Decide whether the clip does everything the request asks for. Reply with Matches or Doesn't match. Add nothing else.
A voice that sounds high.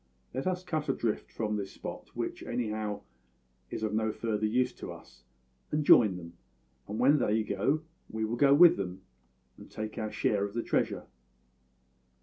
Doesn't match